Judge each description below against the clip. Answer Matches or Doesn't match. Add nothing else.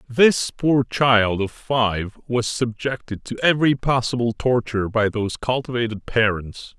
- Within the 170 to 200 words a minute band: Doesn't match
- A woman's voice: Doesn't match